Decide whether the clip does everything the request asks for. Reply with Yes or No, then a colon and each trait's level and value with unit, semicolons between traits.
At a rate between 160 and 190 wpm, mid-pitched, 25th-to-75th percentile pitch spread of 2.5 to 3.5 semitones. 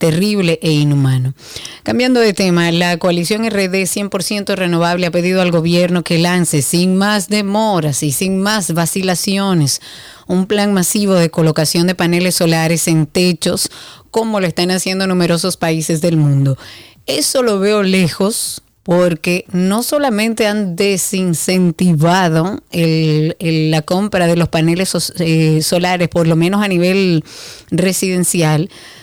No: average, 140 wpm; medium, 180 Hz; average, 2.8 semitones